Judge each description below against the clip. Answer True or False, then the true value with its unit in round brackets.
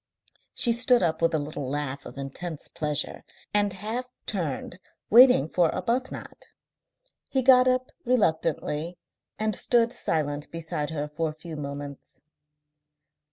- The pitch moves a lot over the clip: True (7.8 semitones)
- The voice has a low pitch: False (165 Hz)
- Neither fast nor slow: False (130 wpm)